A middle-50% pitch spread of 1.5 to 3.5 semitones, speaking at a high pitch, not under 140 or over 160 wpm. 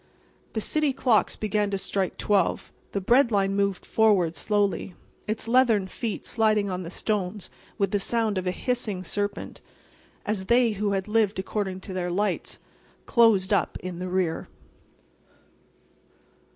Yes: narrow, 2.6 semitones; high, 205 Hz; average, 150 wpm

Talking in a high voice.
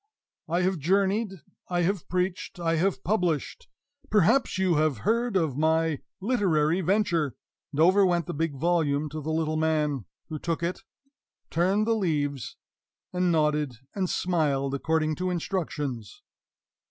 No: medium, 165 Hz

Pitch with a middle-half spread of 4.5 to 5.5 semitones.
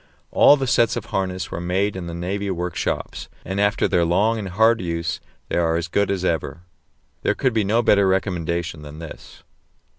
No: average, 3.1 semitones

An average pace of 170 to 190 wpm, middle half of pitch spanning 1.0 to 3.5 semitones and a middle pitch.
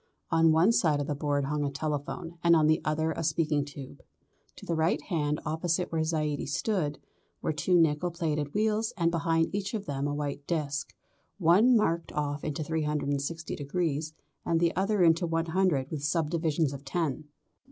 Yes: average, 175 wpm; narrow, 2.5 semitones; medium, 160 Hz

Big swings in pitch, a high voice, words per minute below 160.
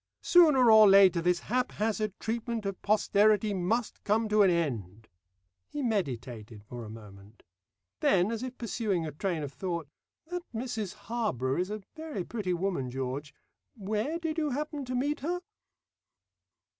Yes: wide, 7.1 semitones; high, 205 Hz; average, 150 wpm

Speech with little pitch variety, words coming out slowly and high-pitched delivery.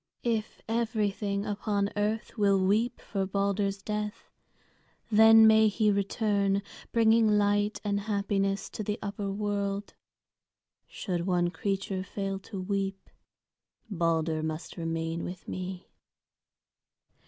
Yes: narrow, 1.5 semitones; slow, 110 wpm; high, 200 Hz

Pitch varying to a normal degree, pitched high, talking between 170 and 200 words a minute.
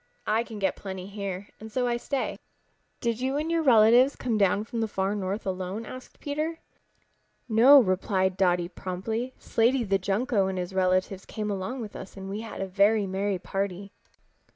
Yes: average, 3.7 semitones; high, 205 Hz; average, 180 wpm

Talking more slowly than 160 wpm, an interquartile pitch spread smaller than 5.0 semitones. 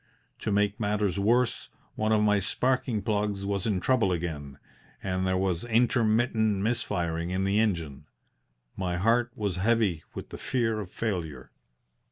Yes: average, 150 wpm; average, 3.4 semitones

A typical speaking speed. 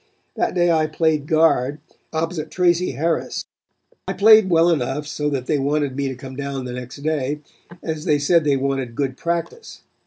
Yes: average, 180 wpm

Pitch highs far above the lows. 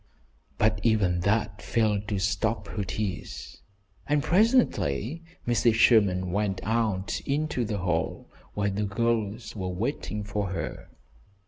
No: average, 3.0 semitones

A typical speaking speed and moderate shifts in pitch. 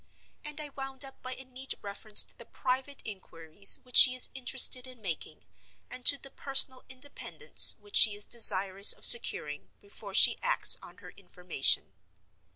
Yes: average, 165 wpm; average, 4.9 semitones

